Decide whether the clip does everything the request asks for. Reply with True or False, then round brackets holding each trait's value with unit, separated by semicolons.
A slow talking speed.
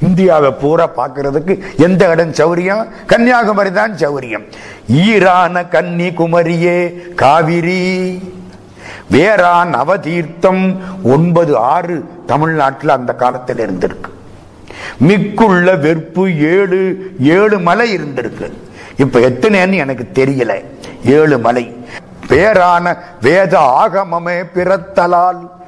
True (70 wpm)